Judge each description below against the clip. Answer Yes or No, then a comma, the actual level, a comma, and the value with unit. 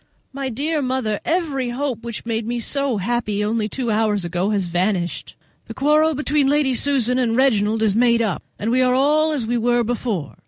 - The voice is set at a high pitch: Yes, high, 240 Hz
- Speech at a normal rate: Yes, average, 195 wpm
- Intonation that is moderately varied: Yes, average, 4.1 semitones